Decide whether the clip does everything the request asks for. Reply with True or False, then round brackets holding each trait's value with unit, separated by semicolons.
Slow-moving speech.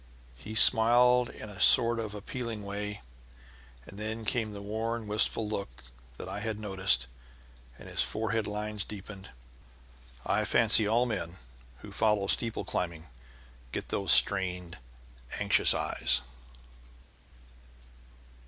True (115 wpm)